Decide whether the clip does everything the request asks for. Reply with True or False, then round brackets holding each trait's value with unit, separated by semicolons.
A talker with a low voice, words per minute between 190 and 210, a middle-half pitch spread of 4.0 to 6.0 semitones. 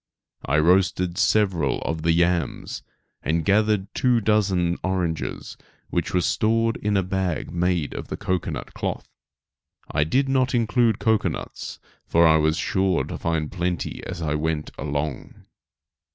False (90 Hz; 140 wpm; 4.4 semitones)